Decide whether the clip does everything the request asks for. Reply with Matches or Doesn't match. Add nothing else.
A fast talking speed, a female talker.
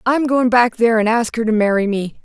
Matches